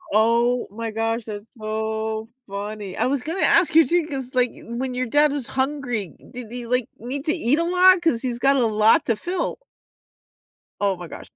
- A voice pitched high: Yes, high, 245 Hz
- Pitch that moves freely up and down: No, average, 4.4 semitones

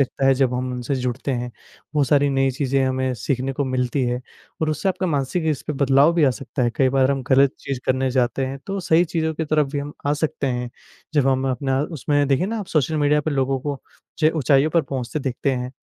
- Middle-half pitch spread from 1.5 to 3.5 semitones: Yes, narrow, 2.4 semitones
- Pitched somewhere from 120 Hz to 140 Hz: Yes, low, 135 Hz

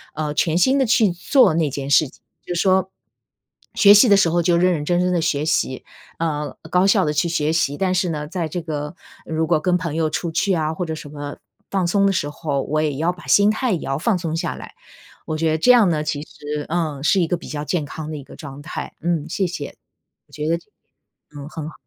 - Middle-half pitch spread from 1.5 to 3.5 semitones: Yes, average, 3.2 semitones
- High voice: No, medium, 165 Hz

